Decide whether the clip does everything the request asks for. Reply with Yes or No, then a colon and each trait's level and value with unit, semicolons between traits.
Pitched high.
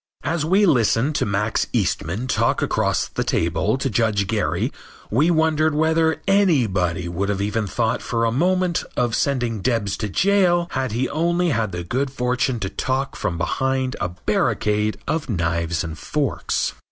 No: low, 120 Hz